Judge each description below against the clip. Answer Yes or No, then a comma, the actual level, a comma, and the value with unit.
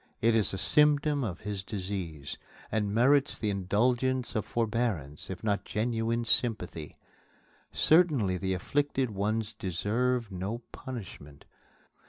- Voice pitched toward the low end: Yes, low, 110 Hz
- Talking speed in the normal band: No, slow, 120 wpm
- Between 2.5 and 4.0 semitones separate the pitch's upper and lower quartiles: No, average, 4.4 semitones